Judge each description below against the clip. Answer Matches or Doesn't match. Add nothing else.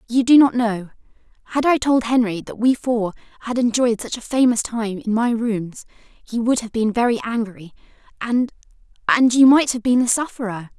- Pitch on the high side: Matches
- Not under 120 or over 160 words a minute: Doesn't match